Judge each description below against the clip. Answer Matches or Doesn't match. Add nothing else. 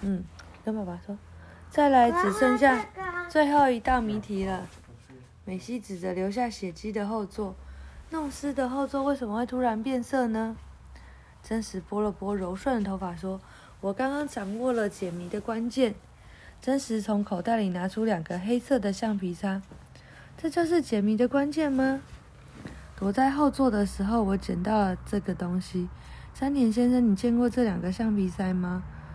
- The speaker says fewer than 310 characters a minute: Matches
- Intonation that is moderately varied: Matches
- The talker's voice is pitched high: Matches